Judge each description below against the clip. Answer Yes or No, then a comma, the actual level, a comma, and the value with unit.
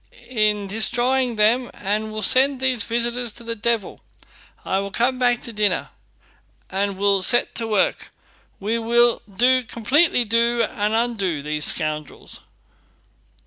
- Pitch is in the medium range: No, high, 230 Hz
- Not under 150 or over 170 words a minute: No, average, 140 wpm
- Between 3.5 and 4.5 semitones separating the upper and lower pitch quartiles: No, average, 3.0 semitones